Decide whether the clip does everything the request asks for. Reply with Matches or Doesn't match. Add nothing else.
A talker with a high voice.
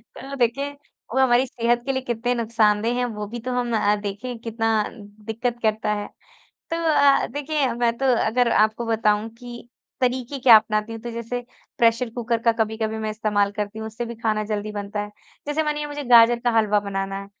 Matches